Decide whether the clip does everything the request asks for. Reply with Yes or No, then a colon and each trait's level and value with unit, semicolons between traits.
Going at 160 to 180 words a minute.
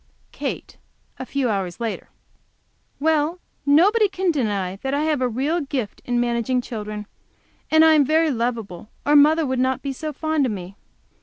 Yes: average, 165 wpm